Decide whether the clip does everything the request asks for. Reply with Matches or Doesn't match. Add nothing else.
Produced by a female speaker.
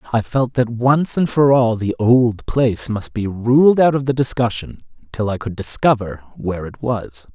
Doesn't match